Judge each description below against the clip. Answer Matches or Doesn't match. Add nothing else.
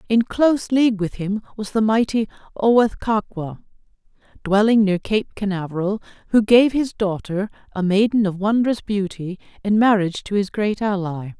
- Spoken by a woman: Matches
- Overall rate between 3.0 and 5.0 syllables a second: Matches